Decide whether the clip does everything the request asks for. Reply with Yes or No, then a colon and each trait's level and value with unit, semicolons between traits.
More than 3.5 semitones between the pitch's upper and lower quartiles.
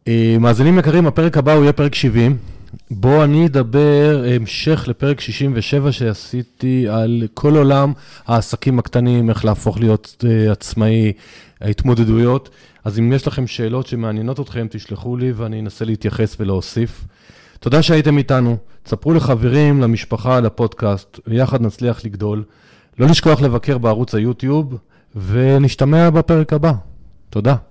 Yes: average, 4.0 semitones